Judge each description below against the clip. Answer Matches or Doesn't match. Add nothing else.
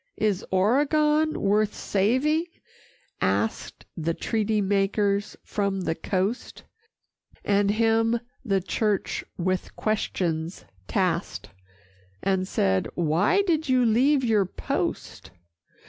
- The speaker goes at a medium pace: Doesn't match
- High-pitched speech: Matches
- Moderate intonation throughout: Matches